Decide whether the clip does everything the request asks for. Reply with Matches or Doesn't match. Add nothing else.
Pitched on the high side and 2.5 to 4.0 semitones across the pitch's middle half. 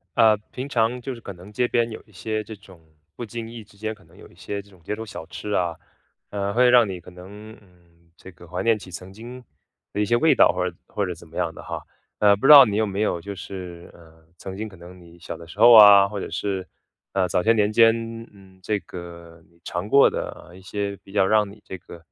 Doesn't match